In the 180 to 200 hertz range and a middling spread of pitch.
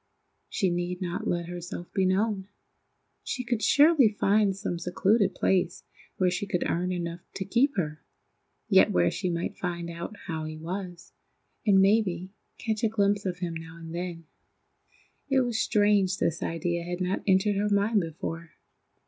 Yes: medium, 185 Hz; average, 3.0 semitones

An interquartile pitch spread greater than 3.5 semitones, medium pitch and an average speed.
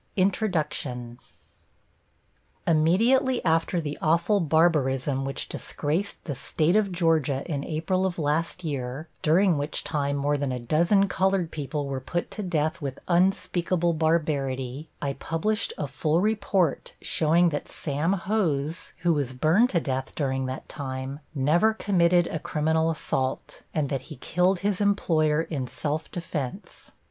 Yes: average, 3.9 semitones; medium, 160 Hz; average, 145 wpm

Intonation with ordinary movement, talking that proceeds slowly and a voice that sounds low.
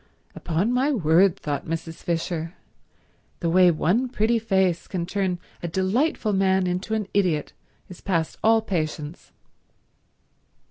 No: average, 4.0 semitones; slow, 130 wpm; medium, 185 Hz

